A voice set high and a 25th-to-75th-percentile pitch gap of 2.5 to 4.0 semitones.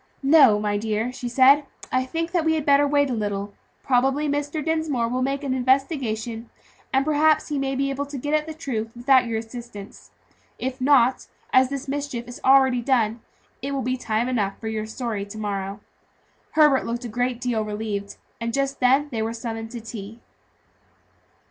Yes: very high, 255 Hz; average, 3.7 semitones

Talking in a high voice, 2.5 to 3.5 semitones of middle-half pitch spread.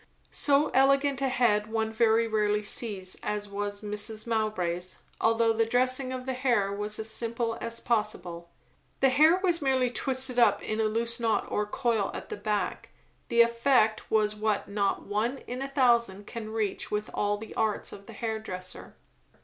Yes: high, 220 Hz; average, 2.9 semitones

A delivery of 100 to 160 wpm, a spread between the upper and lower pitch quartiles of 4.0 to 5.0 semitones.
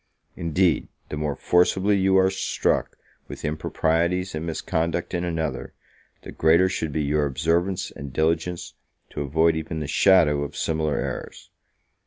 No: average, 145 wpm; average, 2.7 semitones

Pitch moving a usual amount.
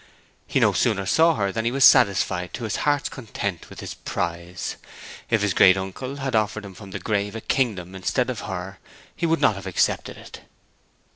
Yes: average, 4.6 semitones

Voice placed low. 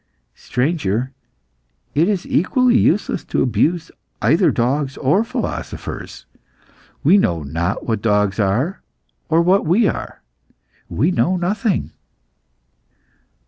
No: medium, 155 Hz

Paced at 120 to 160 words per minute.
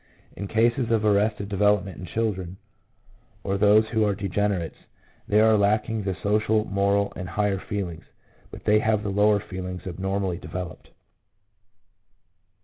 Yes: average, 140 wpm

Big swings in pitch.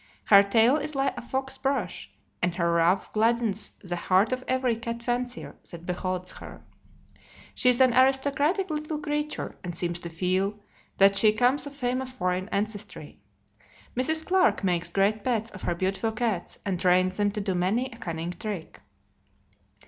Yes: wide, 5.7 semitones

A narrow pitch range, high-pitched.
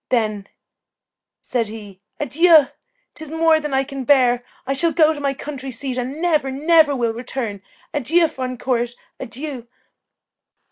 No: average, 4.0 semitones; very high, 270 Hz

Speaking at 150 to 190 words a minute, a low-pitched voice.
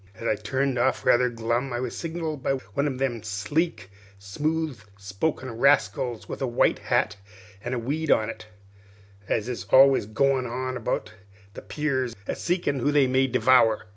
Yes: average, 170 wpm; low, 130 Hz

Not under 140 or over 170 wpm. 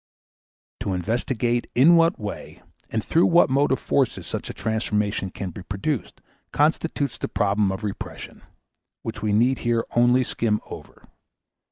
Yes: average, 145 wpm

